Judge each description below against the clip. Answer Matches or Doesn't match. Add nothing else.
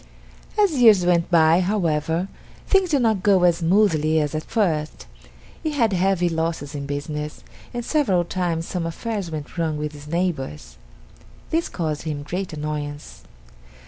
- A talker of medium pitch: Matches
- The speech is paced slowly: Doesn't match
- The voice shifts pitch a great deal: Doesn't match